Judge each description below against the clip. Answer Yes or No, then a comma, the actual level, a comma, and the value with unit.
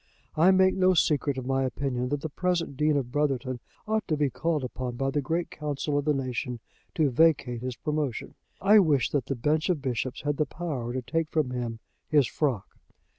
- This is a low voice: No, medium, 145 Hz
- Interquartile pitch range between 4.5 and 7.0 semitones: No, average, 3.6 semitones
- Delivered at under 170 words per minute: No, fast, 205 wpm